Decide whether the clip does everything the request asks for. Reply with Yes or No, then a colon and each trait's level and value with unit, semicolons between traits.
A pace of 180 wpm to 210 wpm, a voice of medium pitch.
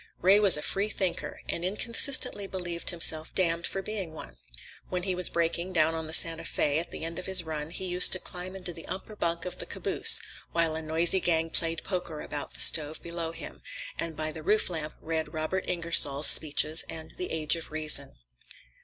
Yes: average, 200 wpm; medium, 170 Hz